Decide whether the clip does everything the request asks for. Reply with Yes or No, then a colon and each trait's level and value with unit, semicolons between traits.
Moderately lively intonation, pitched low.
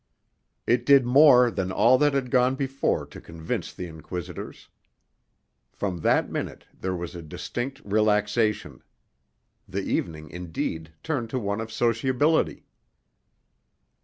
No: wide, 6.3 semitones; low, 110 Hz